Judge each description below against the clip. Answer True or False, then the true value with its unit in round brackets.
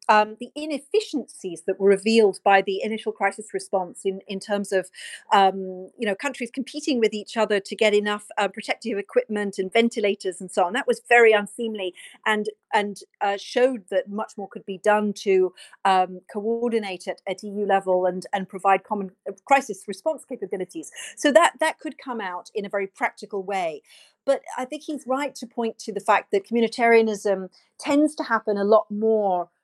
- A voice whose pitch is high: True (210 Hz)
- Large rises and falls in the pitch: False (4.0 semitones)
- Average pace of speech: True (185 wpm)